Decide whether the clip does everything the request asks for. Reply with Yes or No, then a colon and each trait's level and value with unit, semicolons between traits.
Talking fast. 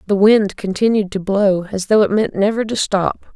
Yes: fast, 215 wpm